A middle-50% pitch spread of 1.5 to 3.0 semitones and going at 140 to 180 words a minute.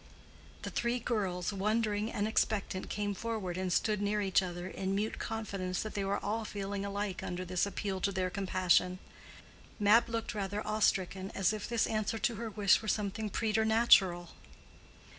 Yes: narrow, 2.5 semitones; average, 170 wpm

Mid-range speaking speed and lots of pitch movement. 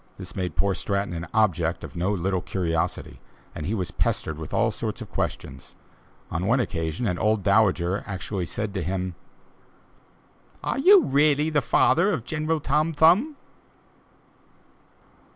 Yes: average, 145 wpm; wide, 8.8 semitones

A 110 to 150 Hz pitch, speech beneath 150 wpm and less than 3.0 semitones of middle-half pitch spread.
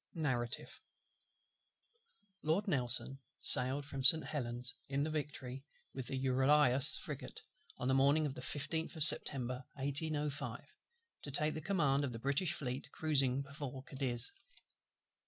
Yes: medium, 140 Hz; slow, 135 wpm; narrow, 2.5 semitones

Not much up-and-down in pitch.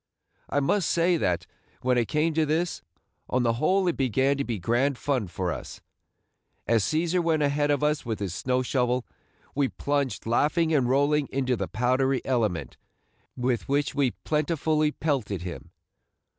No: average, 3.7 semitones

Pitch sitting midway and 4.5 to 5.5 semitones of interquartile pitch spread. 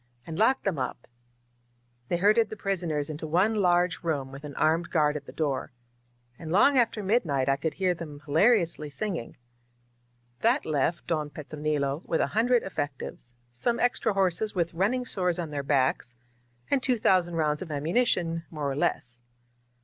Yes: medium, 165 Hz; average, 5.2 semitones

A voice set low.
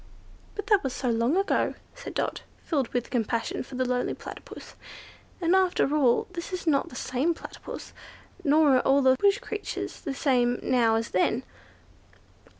No: very high, 270 Hz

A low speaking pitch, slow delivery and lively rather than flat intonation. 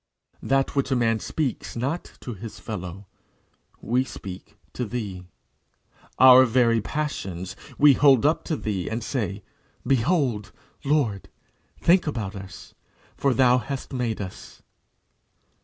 No: low, 120 Hz; slow, 130 wpm; average, 4.8 semitones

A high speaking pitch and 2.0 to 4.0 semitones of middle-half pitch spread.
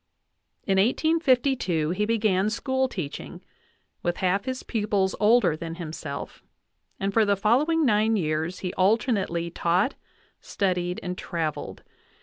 No: high, 195 Hz; average, 4.7 semitones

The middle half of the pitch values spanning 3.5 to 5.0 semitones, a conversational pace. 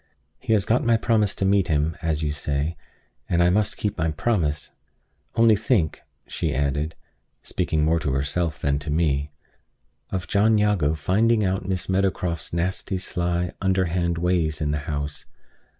Yes: average, 4.3 semitones; average, 160 wpm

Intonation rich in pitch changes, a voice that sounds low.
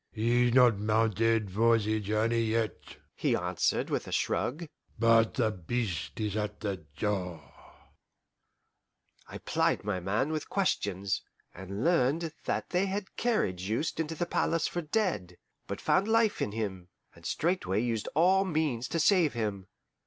Yes: wide, 7.5 semitones; low, 115 Hz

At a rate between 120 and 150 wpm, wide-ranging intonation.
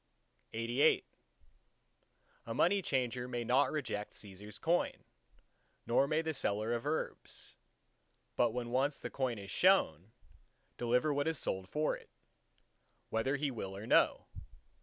No: average, 140 wpm; average, 4.6 semitones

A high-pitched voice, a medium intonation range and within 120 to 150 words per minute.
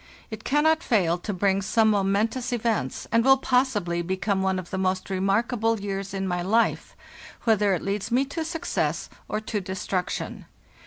No: high, 205 Hz; average, 3.6 semitones; average, 170 wpm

